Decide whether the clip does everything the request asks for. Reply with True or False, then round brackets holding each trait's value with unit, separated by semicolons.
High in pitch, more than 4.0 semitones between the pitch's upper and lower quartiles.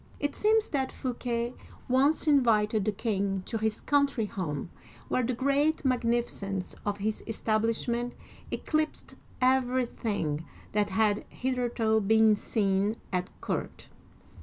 False (230 Hz; 3.7 semitones)